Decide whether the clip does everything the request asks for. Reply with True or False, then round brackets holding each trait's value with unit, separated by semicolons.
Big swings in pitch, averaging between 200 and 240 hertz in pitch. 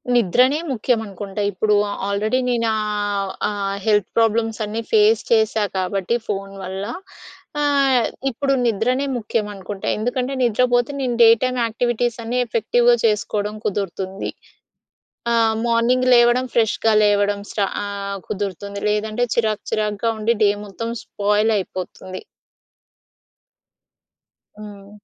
False (2.8 semitones; 215 Hz)